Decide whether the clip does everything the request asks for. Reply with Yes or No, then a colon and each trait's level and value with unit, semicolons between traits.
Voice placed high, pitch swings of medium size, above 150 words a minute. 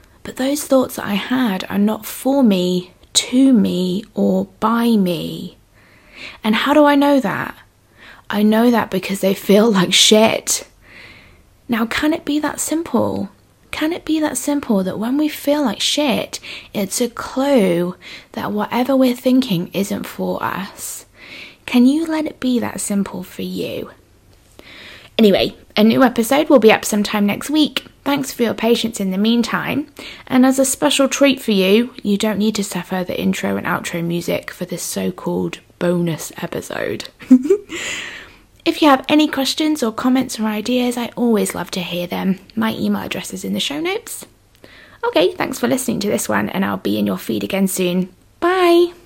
No: high, 230 Hz; wide, 6.1 semitones; average, 175 wpm